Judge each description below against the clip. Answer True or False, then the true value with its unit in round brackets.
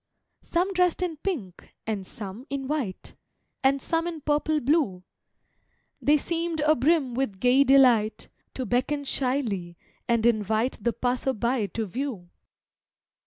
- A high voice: True (260 Hz)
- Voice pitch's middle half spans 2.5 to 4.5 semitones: False (5.3 semitones)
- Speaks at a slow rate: True (130 wpm)